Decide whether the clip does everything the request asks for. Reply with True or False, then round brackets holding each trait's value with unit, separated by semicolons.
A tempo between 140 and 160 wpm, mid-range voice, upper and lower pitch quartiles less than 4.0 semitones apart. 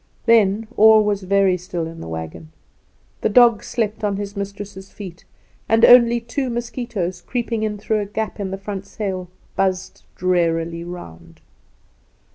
False (150 wpm; 200 Hz; 3.4 semitones)